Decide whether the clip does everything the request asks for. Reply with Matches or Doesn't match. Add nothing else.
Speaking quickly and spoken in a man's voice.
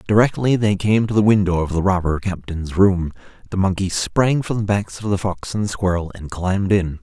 Matches